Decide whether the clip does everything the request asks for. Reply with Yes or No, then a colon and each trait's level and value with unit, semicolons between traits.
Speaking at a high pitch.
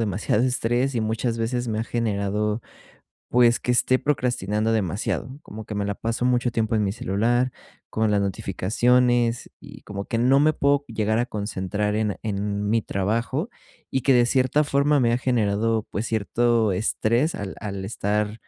No: low, 115 Hz